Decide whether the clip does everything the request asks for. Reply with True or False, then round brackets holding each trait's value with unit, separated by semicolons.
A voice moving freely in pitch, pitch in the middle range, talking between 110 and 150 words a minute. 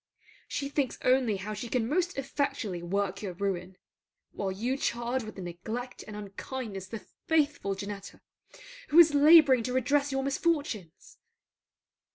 False (5.9 semitones; 235 Hz; 140 wpm)